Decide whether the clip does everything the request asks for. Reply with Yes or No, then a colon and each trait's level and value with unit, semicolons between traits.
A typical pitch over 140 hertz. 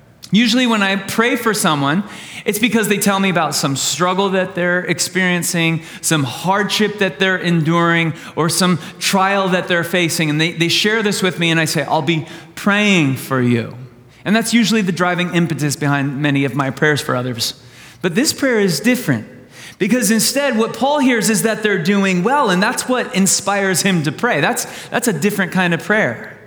Yes: medium, 185 Hz